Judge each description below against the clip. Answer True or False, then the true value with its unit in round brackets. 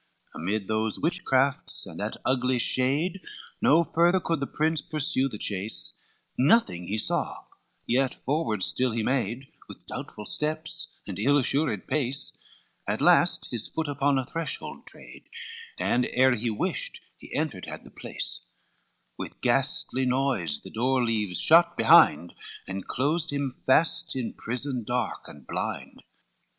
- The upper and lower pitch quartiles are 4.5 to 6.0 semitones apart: True (5.2 semitones)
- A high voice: False (130 Hz)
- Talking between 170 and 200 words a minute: False (145 wpm)